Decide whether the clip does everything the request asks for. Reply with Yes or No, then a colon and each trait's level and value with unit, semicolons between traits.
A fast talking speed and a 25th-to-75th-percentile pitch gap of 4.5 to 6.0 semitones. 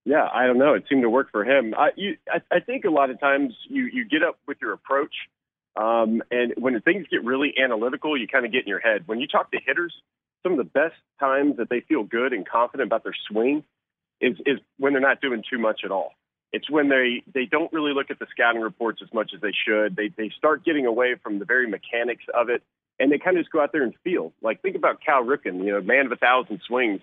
Yes: fast, 260 wpm; wide, 5.6 semitones